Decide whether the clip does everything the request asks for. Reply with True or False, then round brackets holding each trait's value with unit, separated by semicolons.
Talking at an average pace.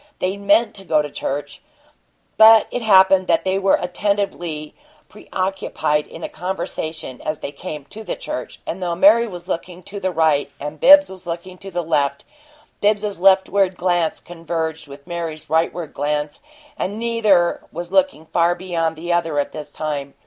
True (170 wpm)